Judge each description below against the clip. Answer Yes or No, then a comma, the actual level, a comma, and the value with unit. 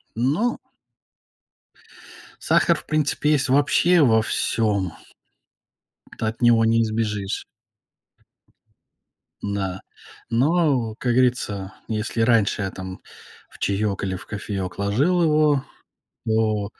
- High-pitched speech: No, low, 115 Hz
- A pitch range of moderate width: Yes, average, 4.9 semitones